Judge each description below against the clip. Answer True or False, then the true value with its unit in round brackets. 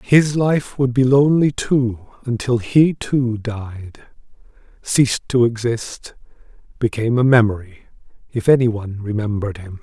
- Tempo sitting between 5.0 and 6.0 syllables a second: False (4.5 syllables/s)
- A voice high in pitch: False (120 Hz)